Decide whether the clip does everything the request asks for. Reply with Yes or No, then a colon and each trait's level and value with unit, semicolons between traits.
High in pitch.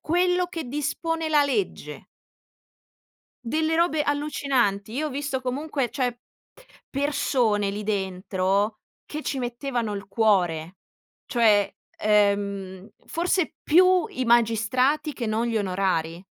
Yes: high, 240 Hz